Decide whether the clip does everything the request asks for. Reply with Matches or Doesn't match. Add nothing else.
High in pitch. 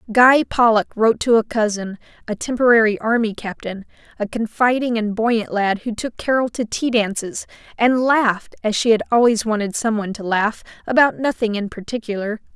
Matches